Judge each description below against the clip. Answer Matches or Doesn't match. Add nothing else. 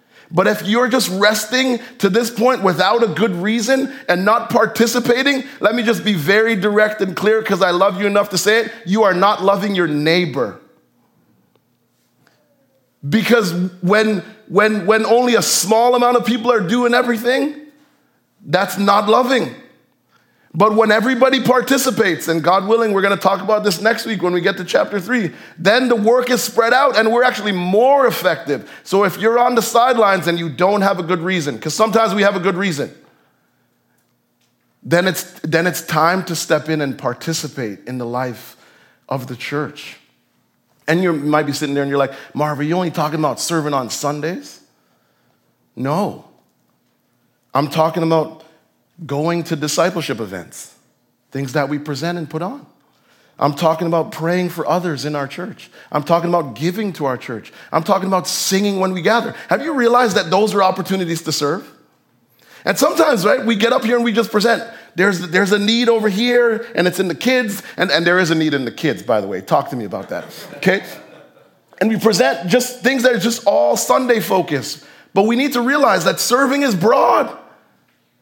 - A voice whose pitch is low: Doesn't match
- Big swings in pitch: Matches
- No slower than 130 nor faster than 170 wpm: Doesn't match